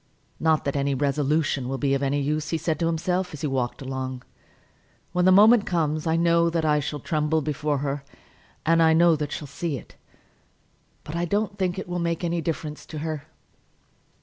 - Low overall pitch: No, medium, 155 Hz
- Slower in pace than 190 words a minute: No, average, 200 wpm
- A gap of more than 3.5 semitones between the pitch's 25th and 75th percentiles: No, average, 2.8 semitones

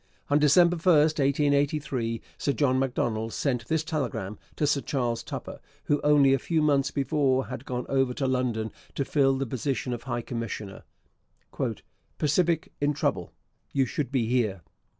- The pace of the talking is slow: No, average, 155 wpm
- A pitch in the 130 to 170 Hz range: Yes, low, 135 Hz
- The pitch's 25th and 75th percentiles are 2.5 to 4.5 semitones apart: Yes, average, 3.1 semitones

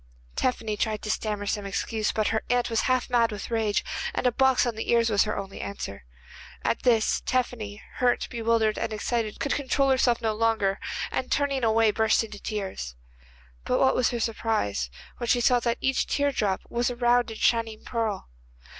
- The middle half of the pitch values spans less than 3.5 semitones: Yes, narrow, 2.4 semitones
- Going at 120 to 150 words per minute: No, average, 190 wpm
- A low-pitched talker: No, high, 225 Hz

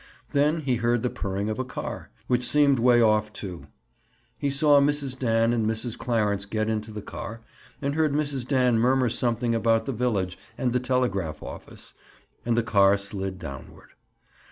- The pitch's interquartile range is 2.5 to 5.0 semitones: Yes, average, 3.3 semitones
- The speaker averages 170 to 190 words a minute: Yes, average, 175 wpm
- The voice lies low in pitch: Yes, low, 115 Hz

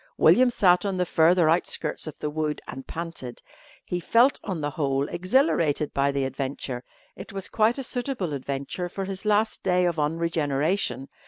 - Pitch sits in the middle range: Yes, medium, 165 Hz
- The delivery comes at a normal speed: Yes, average, 170 wpm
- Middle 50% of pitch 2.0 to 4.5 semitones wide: No, wide, 5.4 semitones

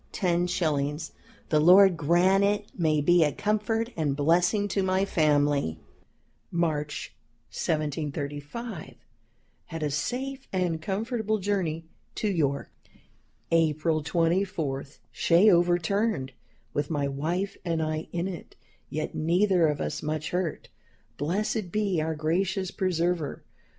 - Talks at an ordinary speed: No, slow, 115 wpm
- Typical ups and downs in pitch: Yes, average, 4.0 semitones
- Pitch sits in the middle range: Yes, medium, 170 Hz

